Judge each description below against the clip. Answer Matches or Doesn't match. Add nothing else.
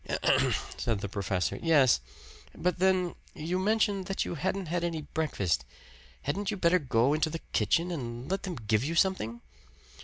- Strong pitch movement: Matches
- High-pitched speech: Doesn't match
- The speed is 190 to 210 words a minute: Doesn't match